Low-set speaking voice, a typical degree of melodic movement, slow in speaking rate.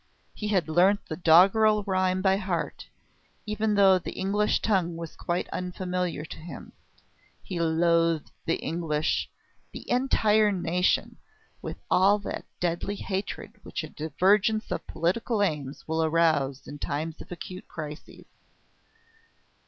No: medium, 180 Hz; average, 3.7 semitones; slow, 130 wpm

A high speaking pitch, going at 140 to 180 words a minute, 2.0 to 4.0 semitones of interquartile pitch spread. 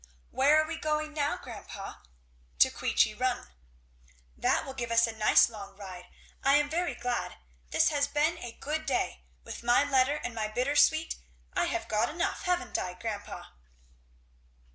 No: very high, 270 Hz; average, 165 wpm; average, 5.2 semitones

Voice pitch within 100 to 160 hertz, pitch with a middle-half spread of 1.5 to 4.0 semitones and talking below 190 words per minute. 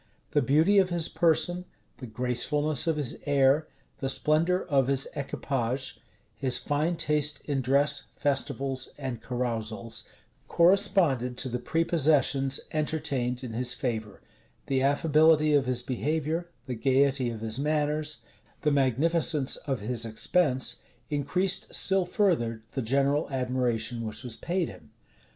Yes: medium, 140 Hz; average, 3.6 semitones; slow, 135 wpm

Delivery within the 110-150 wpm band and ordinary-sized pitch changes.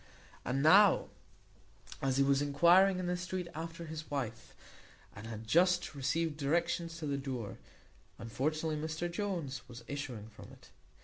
Yes: average, 145 wpm; average, 4.2 semitones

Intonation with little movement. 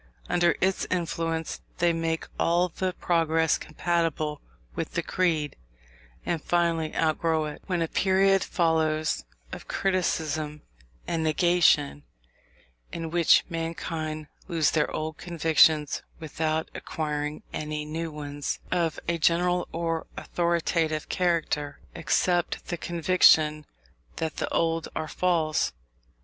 Yes: narrow, 1.9 semitones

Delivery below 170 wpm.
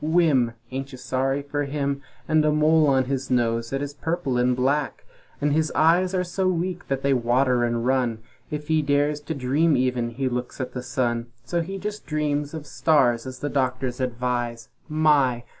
No: average, 190 wpm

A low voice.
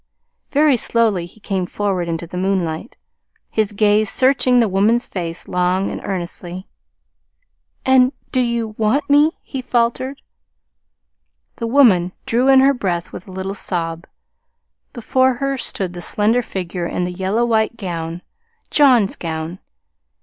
No: high, 205 Hz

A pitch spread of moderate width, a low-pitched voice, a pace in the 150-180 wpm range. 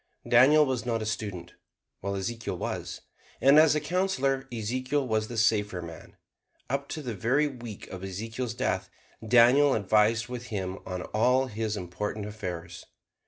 Yes: average, 4.0 semitones; low, 115 Hz; average, 155 wpm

